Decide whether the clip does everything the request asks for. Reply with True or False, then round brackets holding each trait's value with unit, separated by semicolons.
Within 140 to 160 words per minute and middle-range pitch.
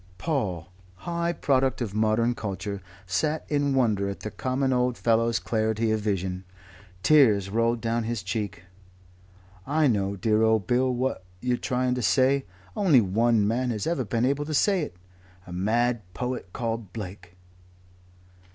False (150 wpm; 115 Hz)